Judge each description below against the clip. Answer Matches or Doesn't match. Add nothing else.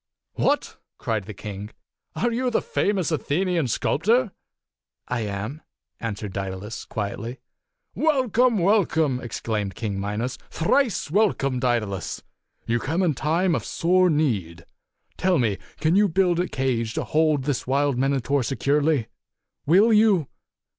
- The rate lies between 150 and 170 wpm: Doesn't match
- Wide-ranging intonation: Matches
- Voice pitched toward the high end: Doesn't match